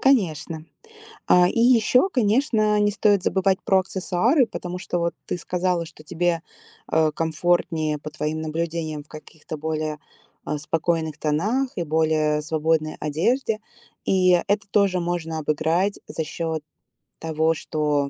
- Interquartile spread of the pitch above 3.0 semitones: Yes, average, 3.6 semitones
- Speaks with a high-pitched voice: No, medium, 165 Hz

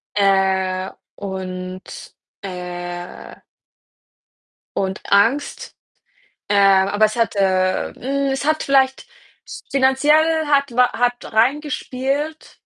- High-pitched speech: Yes, high, 215 Hz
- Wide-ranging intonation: Yes, wide, 6.4 semitones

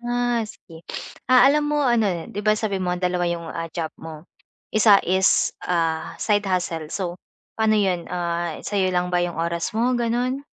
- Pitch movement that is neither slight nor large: Yes, average, 4.9 semitones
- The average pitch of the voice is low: No, high, 190 Hz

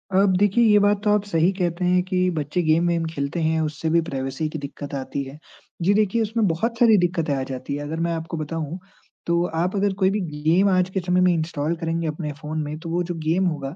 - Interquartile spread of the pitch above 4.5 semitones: No, average, 3.2 semitones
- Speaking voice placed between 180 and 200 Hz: No, medium, 170 Hz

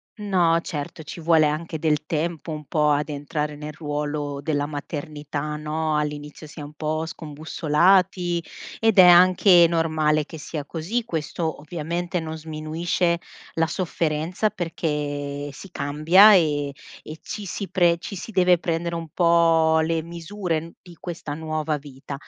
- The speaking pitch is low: No, medium, 160 Hz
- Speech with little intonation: Yes, narrow, 2.3 semitones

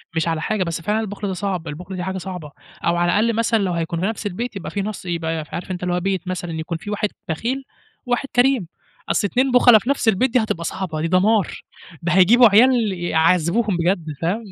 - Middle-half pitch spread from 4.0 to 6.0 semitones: Yes, average, 4.3 semitones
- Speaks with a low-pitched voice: No, high, 190 Hz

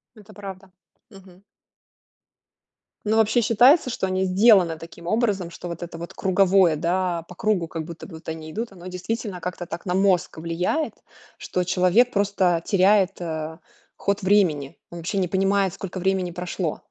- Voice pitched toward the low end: No, medium, 185 Hz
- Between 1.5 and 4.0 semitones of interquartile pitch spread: Yes, narrow, 2.6 semitones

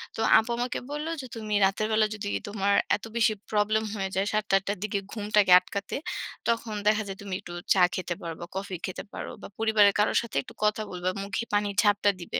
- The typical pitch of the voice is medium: No, high, 205 Hz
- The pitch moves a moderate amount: No, narrow, 1.7 semitones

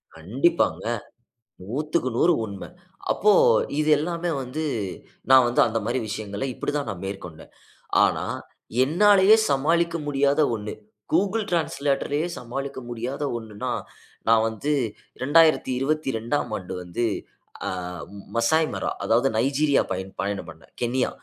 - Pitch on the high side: No, low, 135 Hz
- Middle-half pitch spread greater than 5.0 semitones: Yes, wide, 5.6 semitones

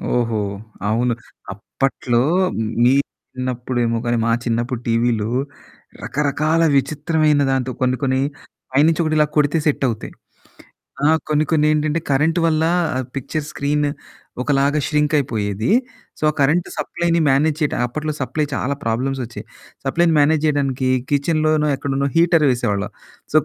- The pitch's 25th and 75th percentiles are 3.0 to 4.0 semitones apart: Yes, average, 3.6 semitones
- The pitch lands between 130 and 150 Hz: Yes, medium, 140 Hz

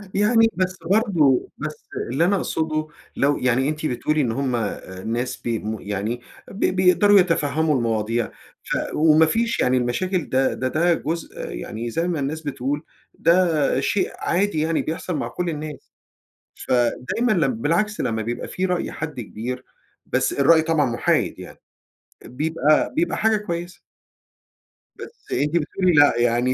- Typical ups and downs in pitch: No, wide, 5.8 semitones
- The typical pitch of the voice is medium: Yes, medium, 155 Hz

